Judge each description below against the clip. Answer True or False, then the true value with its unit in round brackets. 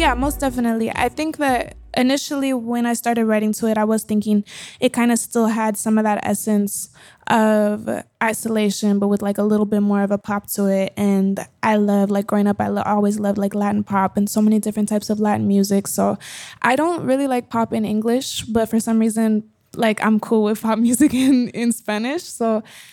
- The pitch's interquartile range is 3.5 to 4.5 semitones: False (2.4 semitones)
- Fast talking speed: True (215 wpm)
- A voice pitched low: False (215 Hz)